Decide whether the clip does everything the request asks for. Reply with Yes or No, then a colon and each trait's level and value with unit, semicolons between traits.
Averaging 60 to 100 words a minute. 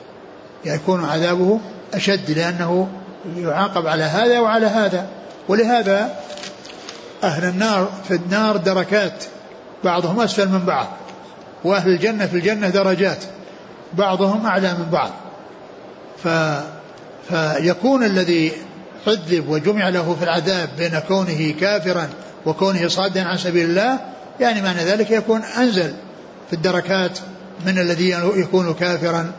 No: average, 110 wpm